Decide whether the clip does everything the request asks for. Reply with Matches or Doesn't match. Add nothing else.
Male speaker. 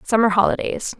Doesn't match